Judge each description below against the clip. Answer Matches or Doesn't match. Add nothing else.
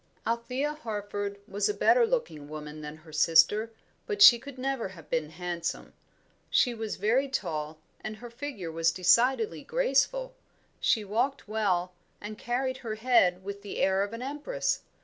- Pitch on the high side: Matches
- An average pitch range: Doesn't match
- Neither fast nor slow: Matches